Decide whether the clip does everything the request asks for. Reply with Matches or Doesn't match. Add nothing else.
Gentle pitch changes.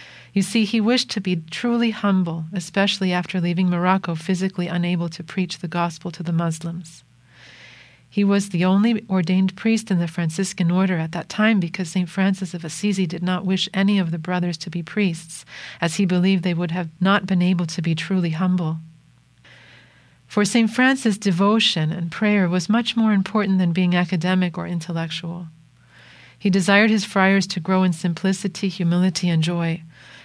Matches